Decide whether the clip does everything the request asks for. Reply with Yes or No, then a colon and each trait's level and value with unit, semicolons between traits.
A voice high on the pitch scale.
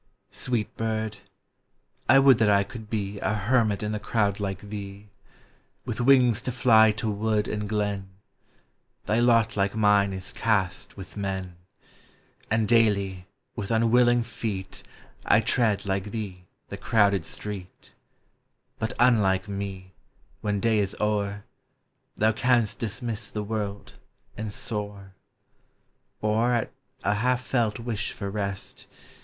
No: low, 105 Hz